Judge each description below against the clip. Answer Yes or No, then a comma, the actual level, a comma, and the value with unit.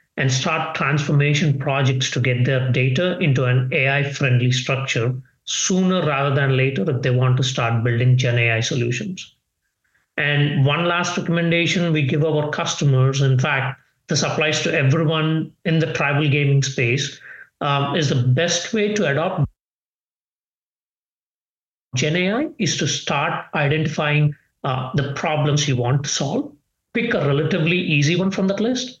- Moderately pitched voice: Yes, medium, 145 Hz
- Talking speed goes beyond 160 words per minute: No, average, 150 wpm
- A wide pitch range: No, average, 3.9 semitones